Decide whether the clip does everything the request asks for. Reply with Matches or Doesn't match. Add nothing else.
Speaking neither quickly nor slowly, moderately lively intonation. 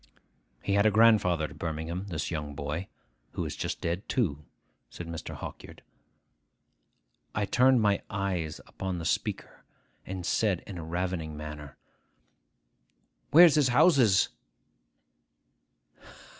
Doesn't match